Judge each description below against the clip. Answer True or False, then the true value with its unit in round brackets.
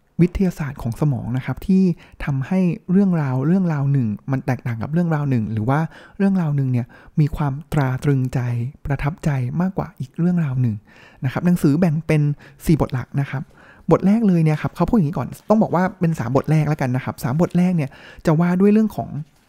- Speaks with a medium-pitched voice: True (150 Hz)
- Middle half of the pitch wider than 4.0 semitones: True (4.5 semitones)